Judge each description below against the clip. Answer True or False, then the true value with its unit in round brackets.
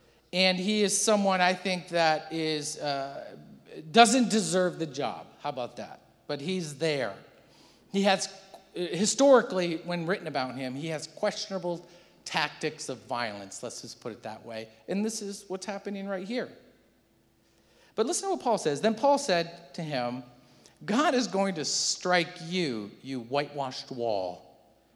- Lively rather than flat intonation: True (6.2 semitones)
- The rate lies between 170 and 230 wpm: False (155 wpm)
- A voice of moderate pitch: True (175 Hz)